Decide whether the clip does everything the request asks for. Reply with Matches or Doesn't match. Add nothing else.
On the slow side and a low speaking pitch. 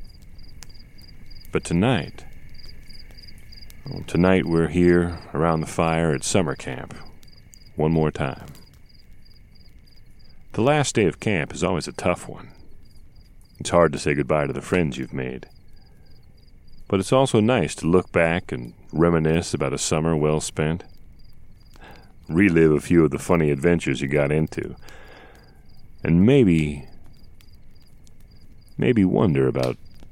Matches